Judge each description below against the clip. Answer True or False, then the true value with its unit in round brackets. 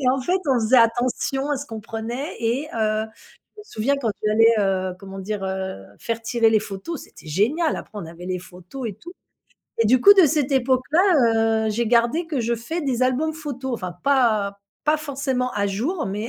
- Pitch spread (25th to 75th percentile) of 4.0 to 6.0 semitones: True (4.5 semitones)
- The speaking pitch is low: False (235 Hz)